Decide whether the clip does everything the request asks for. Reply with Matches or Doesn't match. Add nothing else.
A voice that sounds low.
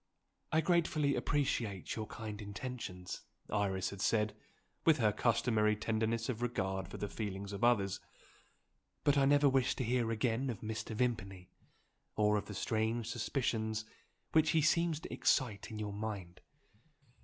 Matches